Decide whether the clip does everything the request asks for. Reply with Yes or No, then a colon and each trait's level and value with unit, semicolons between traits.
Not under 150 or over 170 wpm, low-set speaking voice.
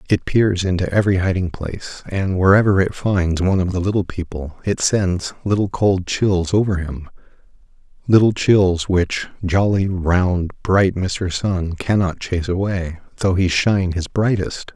Yes: average, 155 wpm; very low, 95 Hz